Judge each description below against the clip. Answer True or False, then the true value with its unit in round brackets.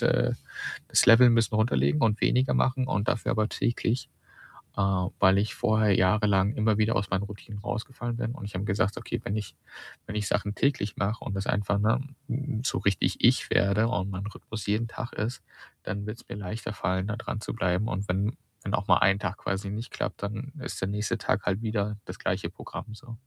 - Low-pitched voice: True (105 Hz)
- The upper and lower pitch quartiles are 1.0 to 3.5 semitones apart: True (2.4 semitones)